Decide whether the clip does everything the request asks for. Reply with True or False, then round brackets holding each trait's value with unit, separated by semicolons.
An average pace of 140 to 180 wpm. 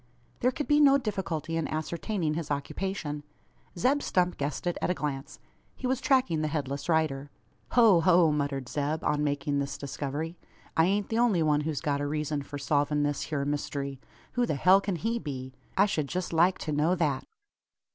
False (190 wpm)